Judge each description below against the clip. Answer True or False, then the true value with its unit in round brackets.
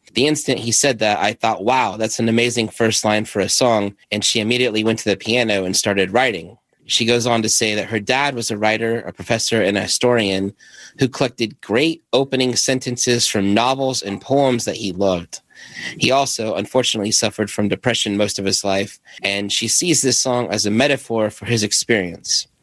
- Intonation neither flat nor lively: True (3.2 semitones)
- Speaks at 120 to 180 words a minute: False (200 wpm)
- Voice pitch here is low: True (115 Hz)